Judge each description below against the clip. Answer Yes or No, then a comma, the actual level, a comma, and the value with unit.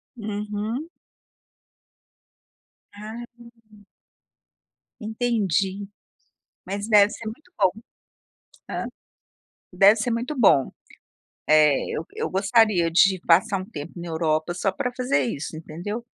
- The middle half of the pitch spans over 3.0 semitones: Yes, average, 4.4 semitones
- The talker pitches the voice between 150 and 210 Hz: Yes, high, 200 Hz